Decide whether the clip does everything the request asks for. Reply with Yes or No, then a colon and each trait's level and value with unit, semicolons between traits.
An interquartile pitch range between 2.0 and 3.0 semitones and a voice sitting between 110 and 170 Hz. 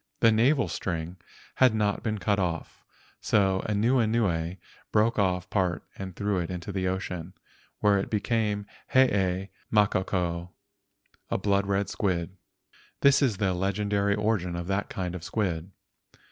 No: average, 2.7 semitones; low, 100 Hz